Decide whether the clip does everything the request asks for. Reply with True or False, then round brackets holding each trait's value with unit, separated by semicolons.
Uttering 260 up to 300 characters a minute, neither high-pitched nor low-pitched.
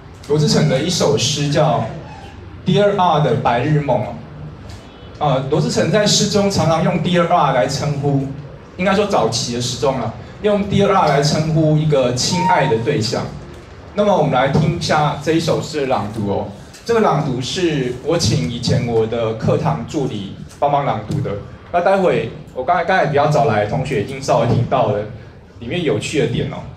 True (285 characters per minute; 145 Hz)